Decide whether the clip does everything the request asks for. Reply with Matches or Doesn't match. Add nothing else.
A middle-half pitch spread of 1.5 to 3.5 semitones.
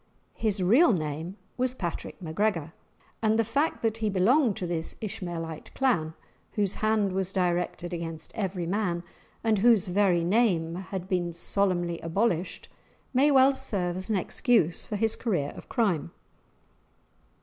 Doesn't match